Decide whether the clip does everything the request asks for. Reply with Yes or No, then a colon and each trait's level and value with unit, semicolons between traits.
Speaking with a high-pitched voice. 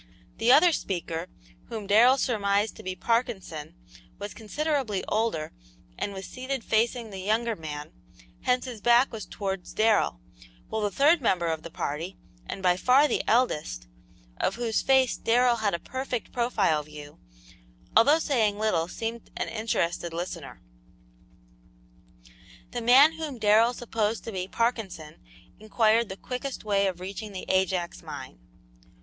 Yes: high, 215 Hz